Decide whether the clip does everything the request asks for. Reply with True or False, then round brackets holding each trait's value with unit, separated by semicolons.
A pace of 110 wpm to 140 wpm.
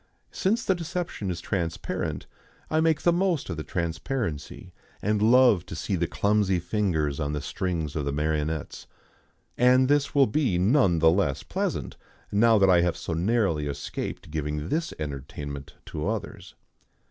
False (160 wpm)